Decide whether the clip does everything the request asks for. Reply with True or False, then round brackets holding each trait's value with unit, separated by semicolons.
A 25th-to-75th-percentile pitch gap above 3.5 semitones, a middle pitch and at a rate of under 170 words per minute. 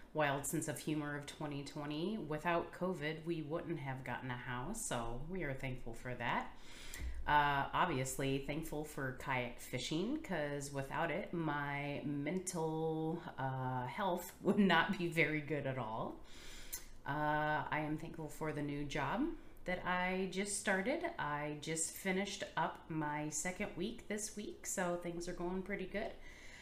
True (3.9 semitones; 155 Hz; 150 wpm)